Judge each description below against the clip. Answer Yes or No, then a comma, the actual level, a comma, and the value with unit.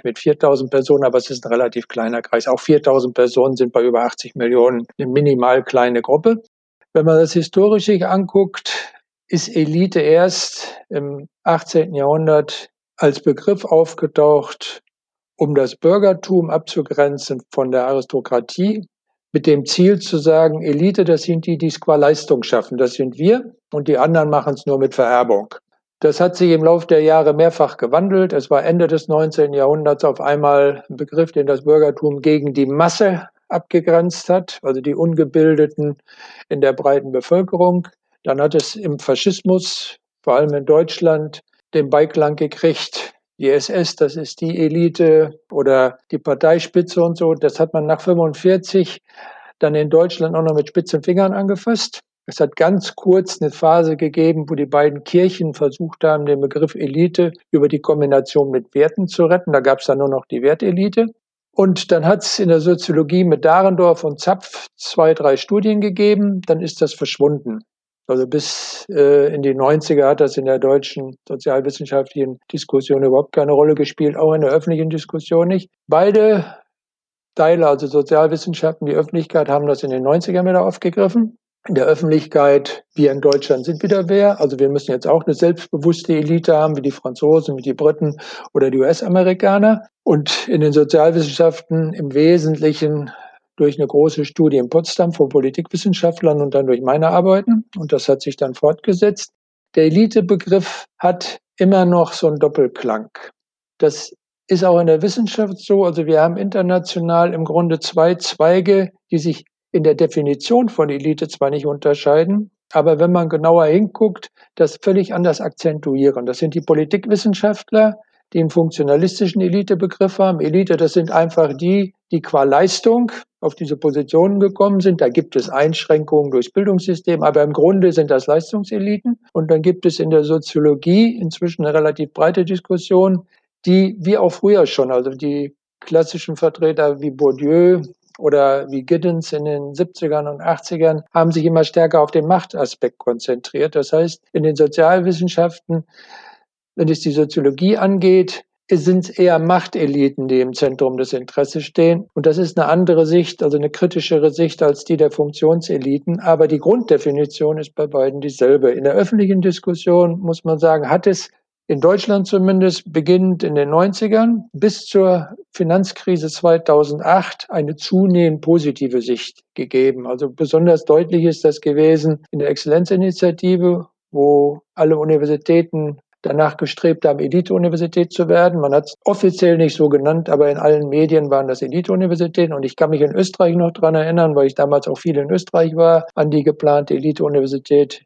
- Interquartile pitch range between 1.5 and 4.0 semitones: Yes, average, 3.7 semitones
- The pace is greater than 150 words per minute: Yes, average, 165 wpm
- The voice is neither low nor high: Yes, medium, 160 Hz